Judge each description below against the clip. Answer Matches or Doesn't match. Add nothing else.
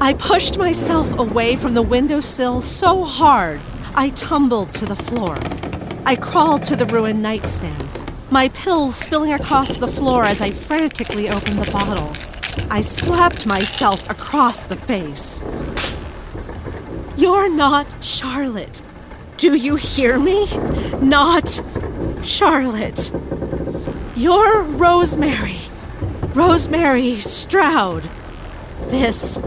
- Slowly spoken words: Matches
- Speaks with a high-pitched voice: Matches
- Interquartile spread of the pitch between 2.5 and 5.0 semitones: Doesn't match